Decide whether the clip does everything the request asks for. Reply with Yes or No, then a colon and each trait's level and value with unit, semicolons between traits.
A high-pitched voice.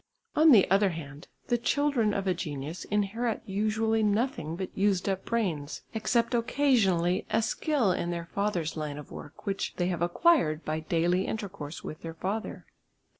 Yes: high, 195 Hz